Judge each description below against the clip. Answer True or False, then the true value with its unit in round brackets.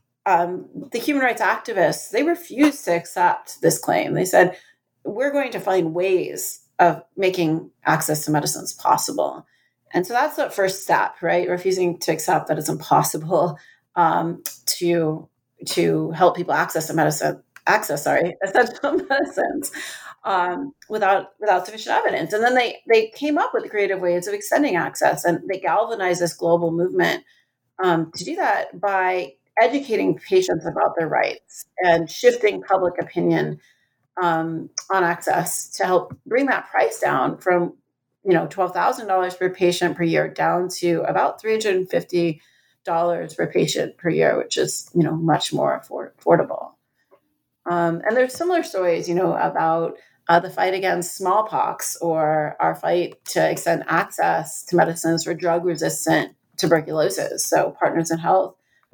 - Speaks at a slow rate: False (150 wpm)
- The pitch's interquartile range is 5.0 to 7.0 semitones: True (5.5 semitones)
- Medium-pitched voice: True (180 Hz)